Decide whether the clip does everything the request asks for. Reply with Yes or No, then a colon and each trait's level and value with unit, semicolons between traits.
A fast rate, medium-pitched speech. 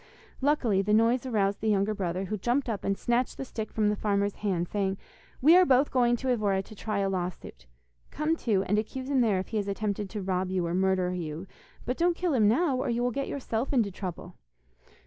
No: fast, 230 wpm; high, 210 Hz